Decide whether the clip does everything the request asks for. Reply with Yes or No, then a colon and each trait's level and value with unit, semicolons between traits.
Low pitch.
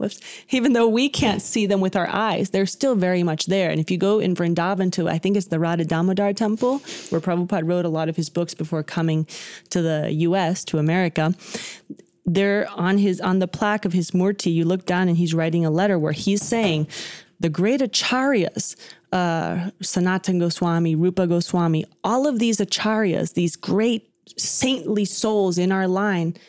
No: medium, 185 Hz